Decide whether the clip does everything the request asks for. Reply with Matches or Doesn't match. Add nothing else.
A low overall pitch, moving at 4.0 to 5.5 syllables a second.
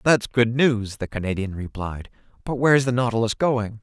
Matches